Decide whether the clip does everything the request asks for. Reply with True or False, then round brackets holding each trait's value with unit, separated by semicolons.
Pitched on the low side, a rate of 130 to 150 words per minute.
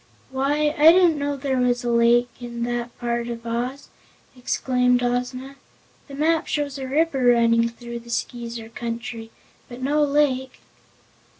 False (250 Hz; 145 wpm)